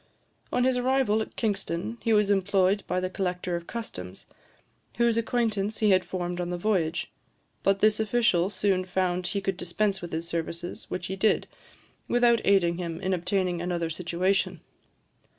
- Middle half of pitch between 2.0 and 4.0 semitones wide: Yes, average, 3.4 semitones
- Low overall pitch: No, high, 190 Hz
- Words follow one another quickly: No, average, 165 wpm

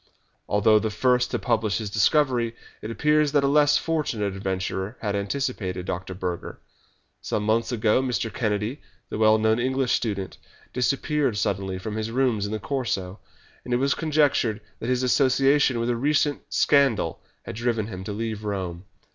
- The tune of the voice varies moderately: Yes, average, 4.4 semitones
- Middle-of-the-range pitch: No, low, 115 Hz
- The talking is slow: No, average, 165 wpm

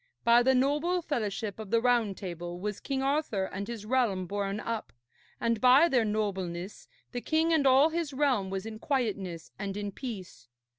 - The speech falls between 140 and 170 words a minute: No, average, 180 wpm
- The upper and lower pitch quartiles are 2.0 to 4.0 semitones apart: No, average, 5.1 semitones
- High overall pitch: Yes, high, 225 Hz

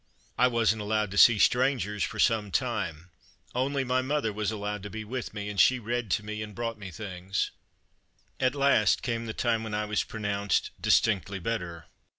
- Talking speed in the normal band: Yes, average, 190 wpm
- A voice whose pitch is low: Yes, low, 110 Hz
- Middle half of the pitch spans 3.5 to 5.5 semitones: No, average, 2.7 semitones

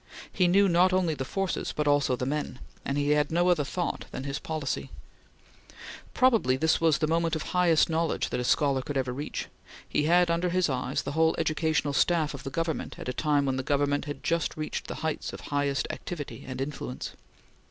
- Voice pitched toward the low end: No, medium, 150 Hz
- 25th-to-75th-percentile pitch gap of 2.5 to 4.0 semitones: Yes, average, 3.1 semitones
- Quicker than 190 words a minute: Yes, fast, 205 wpm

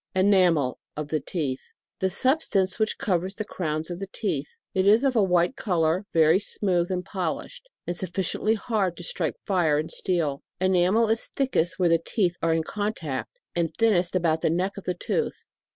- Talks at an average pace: Yes, average, 195 wpm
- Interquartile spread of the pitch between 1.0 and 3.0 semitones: No, average, 3.5 semitones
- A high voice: No, medium, 180 Hz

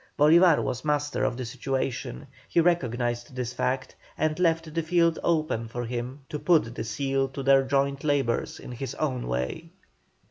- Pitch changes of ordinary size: Yes, average, 4.2 semitones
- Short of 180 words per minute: Yes, average, 170 wpm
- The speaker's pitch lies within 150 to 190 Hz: No, low, 135 Hz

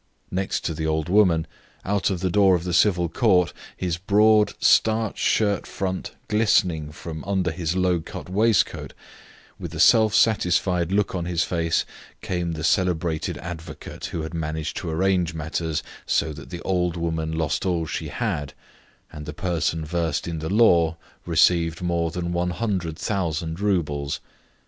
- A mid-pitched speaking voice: No, very low, 85 Hz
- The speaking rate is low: No, average, 155 wpm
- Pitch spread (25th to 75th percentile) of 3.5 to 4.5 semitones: No, average, 2.7 semitones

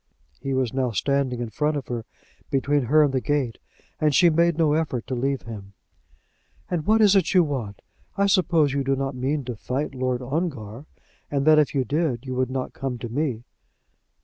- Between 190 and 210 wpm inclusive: Yes, average, 200 wpm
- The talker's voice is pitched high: No, low, 135 Hz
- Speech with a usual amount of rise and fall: Yes, average, 3.4 semitones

